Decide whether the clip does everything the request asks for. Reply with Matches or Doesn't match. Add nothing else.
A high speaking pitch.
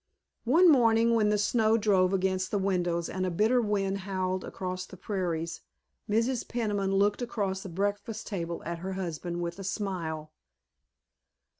Matches